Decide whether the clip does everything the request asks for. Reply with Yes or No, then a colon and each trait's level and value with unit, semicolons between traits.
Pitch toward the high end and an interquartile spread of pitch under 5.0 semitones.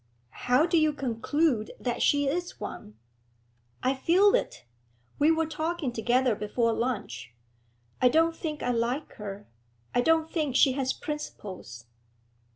No: very high, 265 Hz; average, 5.3 semitones